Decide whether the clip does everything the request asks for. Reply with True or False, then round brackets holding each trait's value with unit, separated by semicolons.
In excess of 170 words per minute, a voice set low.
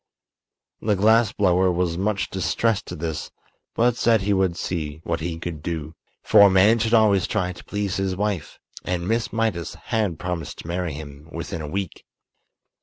True (180 wpm; 95 Hz)